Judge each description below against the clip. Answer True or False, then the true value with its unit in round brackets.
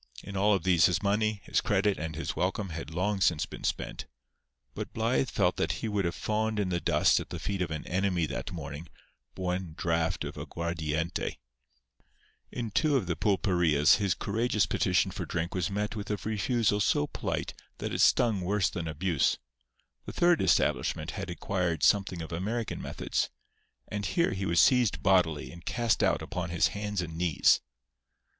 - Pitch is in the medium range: False (95 Hz)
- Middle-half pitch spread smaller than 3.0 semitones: False (3.6 semitones)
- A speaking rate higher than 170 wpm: True (180 wpm)